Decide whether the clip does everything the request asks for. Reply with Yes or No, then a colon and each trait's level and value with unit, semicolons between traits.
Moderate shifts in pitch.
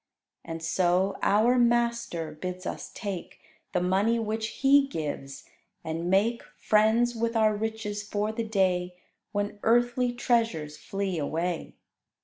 Yes: average, 4.5 semitones